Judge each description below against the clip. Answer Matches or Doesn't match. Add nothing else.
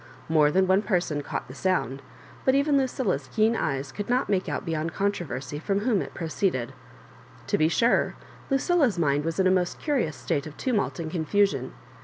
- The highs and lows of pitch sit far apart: Matches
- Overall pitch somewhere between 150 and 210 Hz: Matches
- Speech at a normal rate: Matches